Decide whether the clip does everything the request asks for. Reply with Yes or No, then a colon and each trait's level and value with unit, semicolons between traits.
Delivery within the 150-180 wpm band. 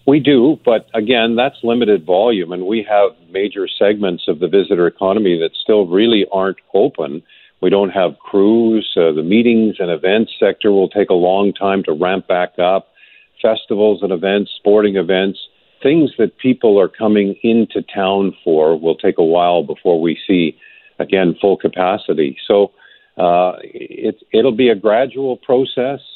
Yes: average, 165 wpm